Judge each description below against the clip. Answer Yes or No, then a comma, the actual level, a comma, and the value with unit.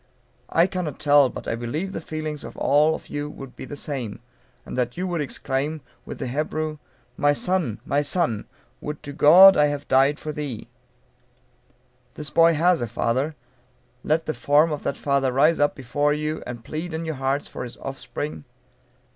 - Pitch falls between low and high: Yes, medium, 145 Hz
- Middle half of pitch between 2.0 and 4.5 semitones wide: Yes, narrow, 2.5 semitones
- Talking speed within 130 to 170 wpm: No, average, 185 wpm